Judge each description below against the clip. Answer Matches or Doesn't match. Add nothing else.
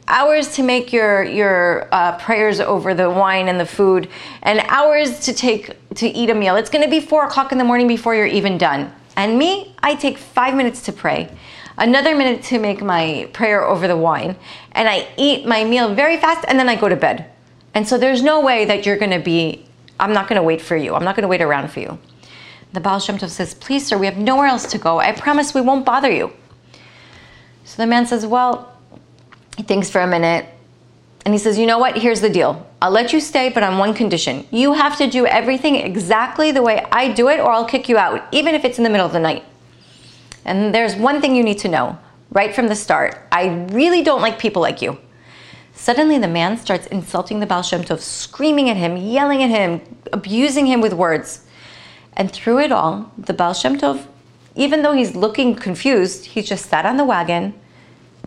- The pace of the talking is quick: Matches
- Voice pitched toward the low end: Doesn't match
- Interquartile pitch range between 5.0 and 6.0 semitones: Matches